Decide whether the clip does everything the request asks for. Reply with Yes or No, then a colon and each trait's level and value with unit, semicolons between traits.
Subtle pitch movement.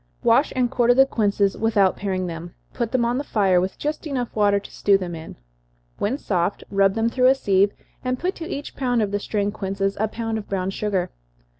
No: average, 3.8 semitones